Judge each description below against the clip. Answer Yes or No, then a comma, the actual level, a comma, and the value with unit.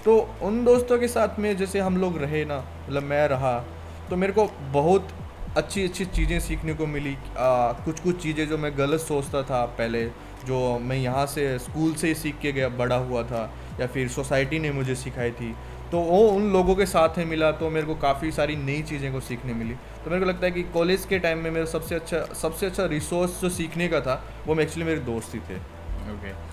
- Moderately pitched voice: Yes, medium, 155 Hz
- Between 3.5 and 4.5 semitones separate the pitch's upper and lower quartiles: No, average, 5.2 semitones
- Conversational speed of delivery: No, fast, 225 wpm